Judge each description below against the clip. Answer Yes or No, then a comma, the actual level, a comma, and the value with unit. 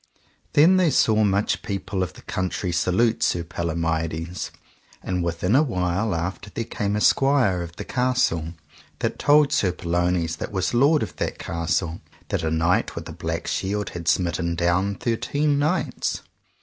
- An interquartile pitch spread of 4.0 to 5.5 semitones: Yes, average, 5.2 semitones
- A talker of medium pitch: No, very low, 95 Hz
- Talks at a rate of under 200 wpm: Yes, average, 160 wpm